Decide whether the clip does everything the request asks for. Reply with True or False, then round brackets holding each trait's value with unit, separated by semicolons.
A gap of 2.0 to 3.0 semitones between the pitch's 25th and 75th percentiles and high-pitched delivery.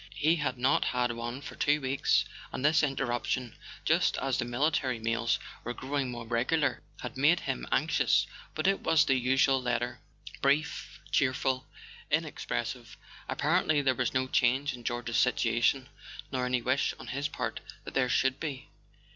False (2.6 semitones; 130 Hz)